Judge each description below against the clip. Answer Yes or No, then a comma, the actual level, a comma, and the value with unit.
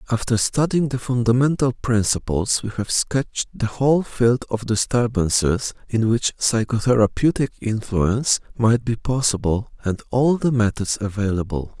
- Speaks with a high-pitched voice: No, low, 115 Hz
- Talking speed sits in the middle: No, slow, 125 wpm